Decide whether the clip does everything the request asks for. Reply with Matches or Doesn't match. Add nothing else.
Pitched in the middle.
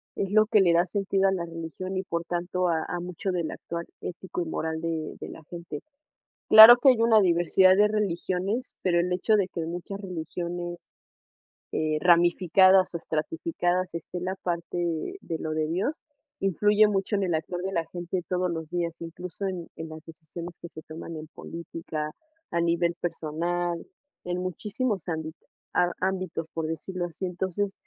Matches